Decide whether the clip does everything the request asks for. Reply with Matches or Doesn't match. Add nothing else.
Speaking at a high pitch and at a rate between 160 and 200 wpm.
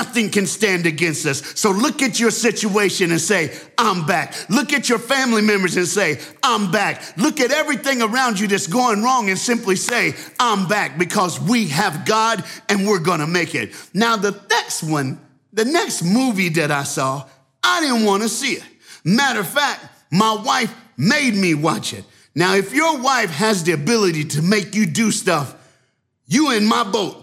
Matches